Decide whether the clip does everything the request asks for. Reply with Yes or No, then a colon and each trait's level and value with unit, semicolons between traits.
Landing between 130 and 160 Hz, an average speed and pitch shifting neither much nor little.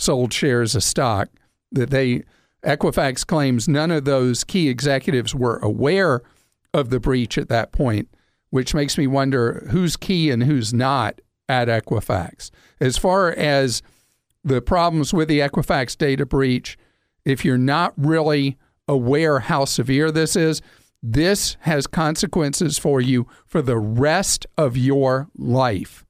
Yes: medium, 140 Hz; average, 145 wpm; average, 3.7 semitones